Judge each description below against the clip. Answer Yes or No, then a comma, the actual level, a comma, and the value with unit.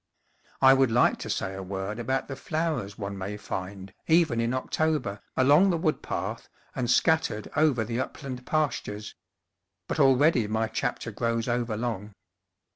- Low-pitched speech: Yes, low, 120 Hz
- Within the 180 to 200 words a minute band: No, average, 155 wpm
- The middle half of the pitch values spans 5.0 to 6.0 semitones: Yes, wide, 5.4 semitones